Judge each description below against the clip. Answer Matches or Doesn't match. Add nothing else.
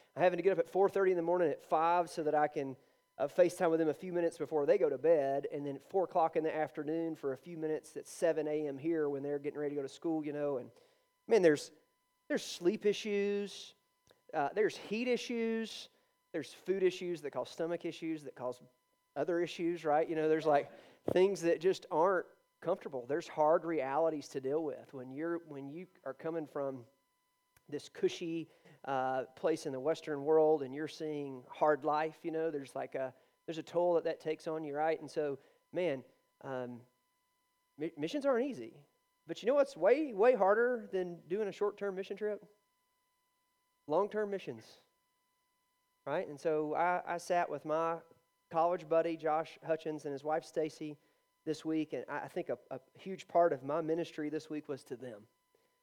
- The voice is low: Doesn't match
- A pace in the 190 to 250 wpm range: Matches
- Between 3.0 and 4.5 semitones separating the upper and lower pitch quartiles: Doesn't match